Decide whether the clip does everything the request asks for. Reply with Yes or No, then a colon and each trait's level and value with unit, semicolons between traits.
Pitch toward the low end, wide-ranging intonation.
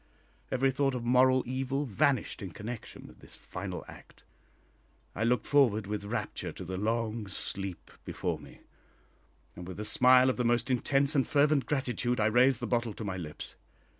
No: low, 120 Hz; average, 3.7 semitones